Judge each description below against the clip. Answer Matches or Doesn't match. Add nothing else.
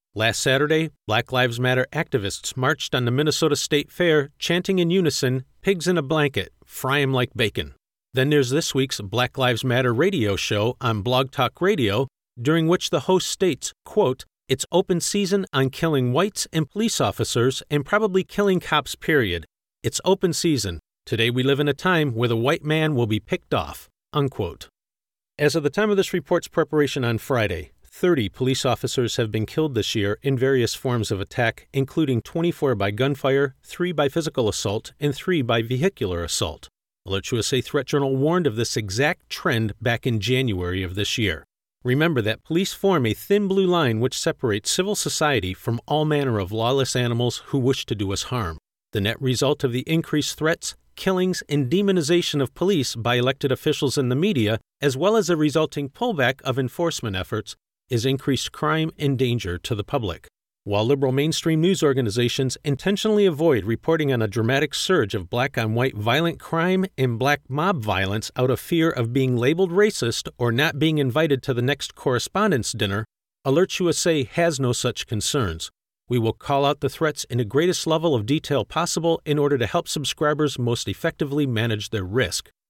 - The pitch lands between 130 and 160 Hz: Matches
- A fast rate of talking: Doesn't match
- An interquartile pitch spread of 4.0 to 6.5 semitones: Matches